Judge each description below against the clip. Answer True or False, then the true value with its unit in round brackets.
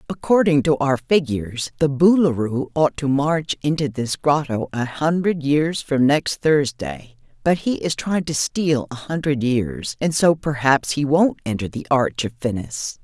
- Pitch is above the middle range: False (145 Hz)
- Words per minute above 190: False (170 wpm)